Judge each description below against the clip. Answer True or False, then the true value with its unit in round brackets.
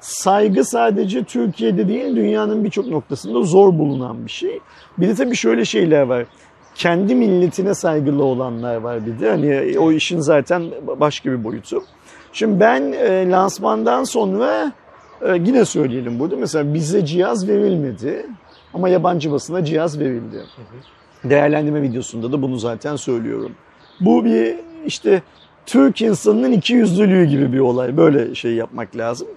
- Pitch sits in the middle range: True (160 Hz)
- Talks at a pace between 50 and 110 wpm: False (135 wpm)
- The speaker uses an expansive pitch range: True (7.9 semitones)